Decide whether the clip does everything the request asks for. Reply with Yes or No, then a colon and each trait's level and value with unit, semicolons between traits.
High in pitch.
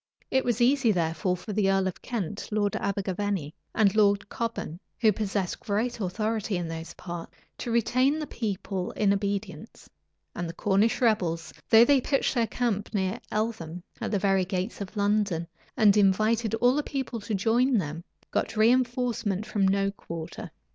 Yes: high, 205 Hz